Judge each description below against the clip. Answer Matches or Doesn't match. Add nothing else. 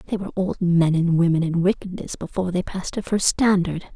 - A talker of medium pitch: Matches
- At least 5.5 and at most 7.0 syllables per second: Matches